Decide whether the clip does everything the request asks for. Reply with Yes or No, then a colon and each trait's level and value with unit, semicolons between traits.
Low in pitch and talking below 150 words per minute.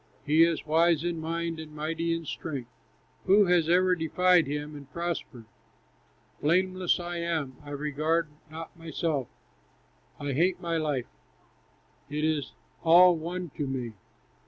No: medium, 165 Hz; slow, 135 wpm